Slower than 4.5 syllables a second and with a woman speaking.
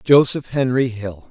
No: 4.1 syllables/s; male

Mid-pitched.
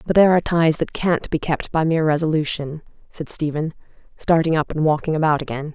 Yes: medium, 155 Hz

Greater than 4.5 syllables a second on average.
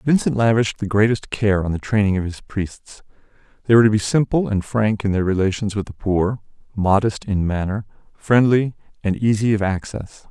Yes: 5.3 syllables/s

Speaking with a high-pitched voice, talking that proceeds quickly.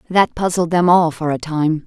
No: medium, 165 Hz; fast, 225 wpm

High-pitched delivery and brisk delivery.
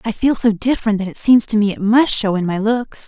Yes: high, 220 Hz; fast, 295 wpm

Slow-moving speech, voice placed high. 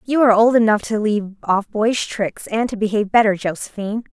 No: average, 200 wpm; high, 215 Hz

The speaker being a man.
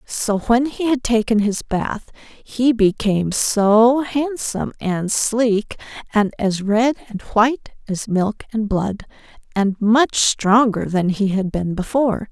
No: female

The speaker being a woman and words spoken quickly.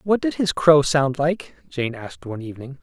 No: male; fast, 210 wpm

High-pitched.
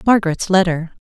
No: medium, 180 Hz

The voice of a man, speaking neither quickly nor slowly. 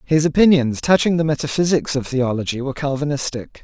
Yes: male; average, 150 wpm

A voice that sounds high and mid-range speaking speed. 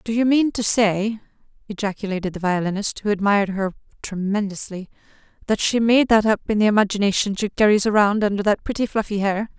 Yes: high, 205 Hz; average, 175 wpm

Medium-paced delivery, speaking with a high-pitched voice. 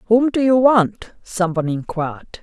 Yes: average, 150 wpm; high, 200 Hz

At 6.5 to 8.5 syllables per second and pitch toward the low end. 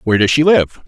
Yes: 6.7 syllables/s; low, 130 Hz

